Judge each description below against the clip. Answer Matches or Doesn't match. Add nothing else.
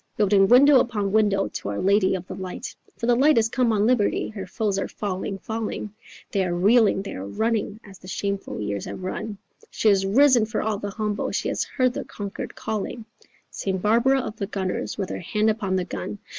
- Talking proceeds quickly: Matches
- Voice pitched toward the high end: Matches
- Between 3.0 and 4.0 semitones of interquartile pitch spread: Doesn't match